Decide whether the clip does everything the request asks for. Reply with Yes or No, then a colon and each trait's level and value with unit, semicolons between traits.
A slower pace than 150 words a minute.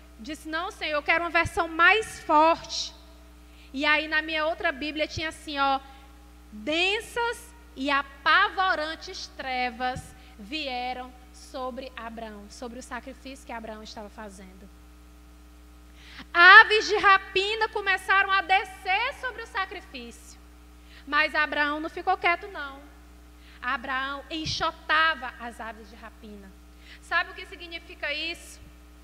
Yes: slow, 120 wpm